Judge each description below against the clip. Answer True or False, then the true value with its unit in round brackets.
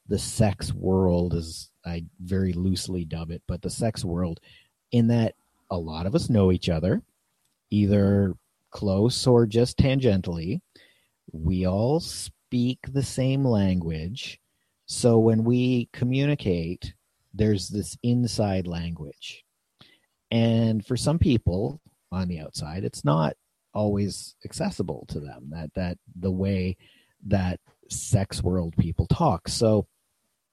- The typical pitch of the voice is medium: False (100 Hz)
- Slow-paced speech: True (125 wpm)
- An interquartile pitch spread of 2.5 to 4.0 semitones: False (4.7 semitones)